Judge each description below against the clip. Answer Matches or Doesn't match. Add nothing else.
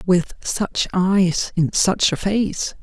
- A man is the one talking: Doesn't match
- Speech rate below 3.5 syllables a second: Matches